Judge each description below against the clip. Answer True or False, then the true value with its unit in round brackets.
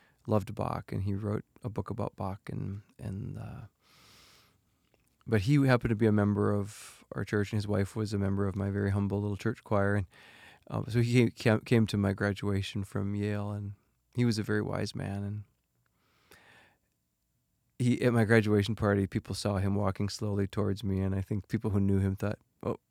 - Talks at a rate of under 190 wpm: False (195 wpm)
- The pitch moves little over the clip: True (2.1 semitones)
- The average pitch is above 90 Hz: True (105 Hz)